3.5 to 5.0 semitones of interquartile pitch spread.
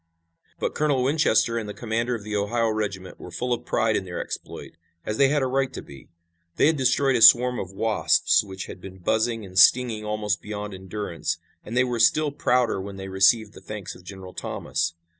Yes: average, 4.2 semitones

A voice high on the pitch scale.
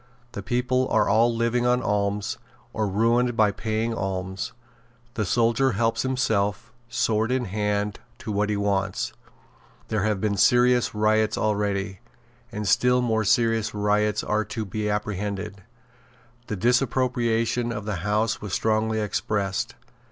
No: low, 110 Hz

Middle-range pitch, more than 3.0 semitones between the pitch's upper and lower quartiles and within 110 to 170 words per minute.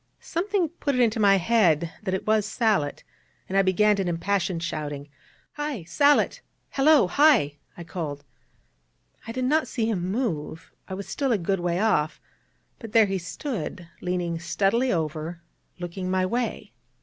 No: high, 195 Hz; wide, 5.5 semitones; average, 160 wpm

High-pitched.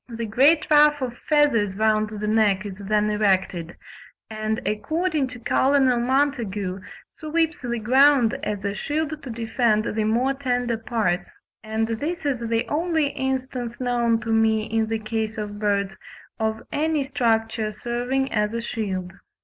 Yes: high, 230 Hz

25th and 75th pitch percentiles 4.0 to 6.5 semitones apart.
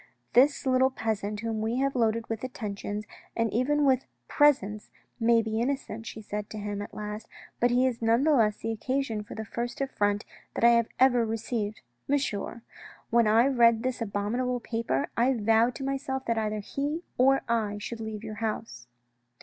No: average, 3.1 semitones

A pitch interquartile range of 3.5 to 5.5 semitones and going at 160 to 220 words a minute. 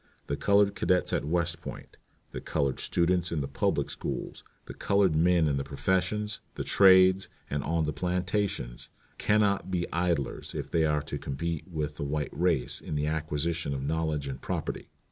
Yes: average, 3.9 semitones; average, 180 wpm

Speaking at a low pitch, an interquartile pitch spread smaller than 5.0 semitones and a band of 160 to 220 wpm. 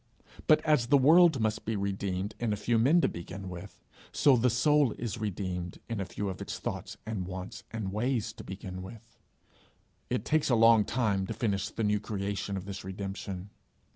Yes: low, 105 Hz; average, 3.5 semitones; average, 195 wpm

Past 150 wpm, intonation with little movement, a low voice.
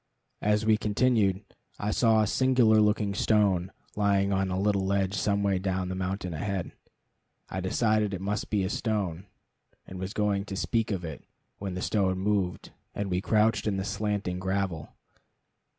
Yes: average, 170 wpm; narrow, 2.0 semitones; low, 100 Hz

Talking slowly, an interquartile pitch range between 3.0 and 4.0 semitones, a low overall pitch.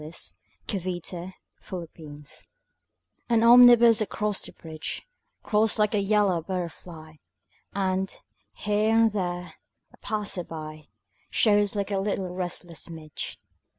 No: slow, 115 wpm; average, 3.4 semitones; high, 190 Hz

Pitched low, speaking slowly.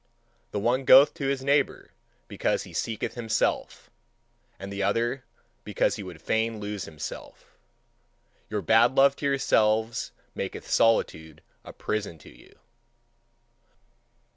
Yes: low, 110 Hz; slow, 125 wpm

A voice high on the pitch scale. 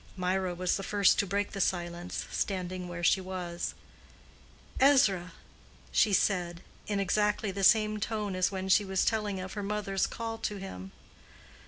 Yes: high, 195 Hz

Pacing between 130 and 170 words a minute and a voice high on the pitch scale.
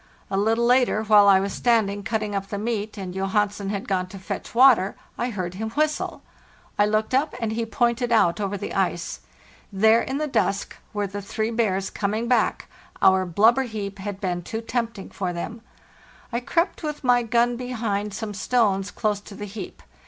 No: average, 185 wpm; high, 210 Hz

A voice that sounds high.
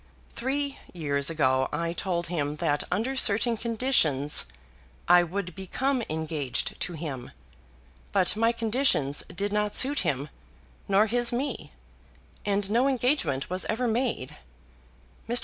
Yes: high, 200 Hz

